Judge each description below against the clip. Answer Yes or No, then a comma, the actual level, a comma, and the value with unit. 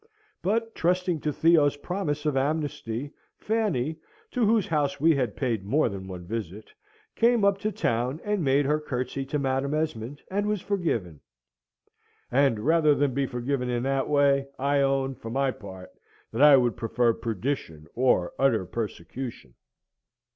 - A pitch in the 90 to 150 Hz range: Yes, medium, 140 Hz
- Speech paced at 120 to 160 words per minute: Yes, average, 155 wpm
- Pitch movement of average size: Yes, average, 4.7 semitones